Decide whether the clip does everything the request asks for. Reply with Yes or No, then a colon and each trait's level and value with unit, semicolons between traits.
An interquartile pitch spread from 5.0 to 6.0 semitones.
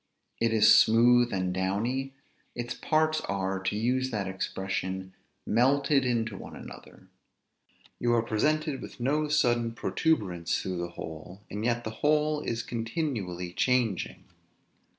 Yes: wide, 5.4 semitones